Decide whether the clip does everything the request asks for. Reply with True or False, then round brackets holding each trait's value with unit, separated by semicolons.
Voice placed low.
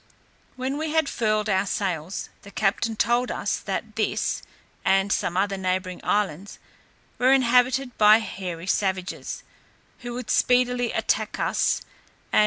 False (210 Hz)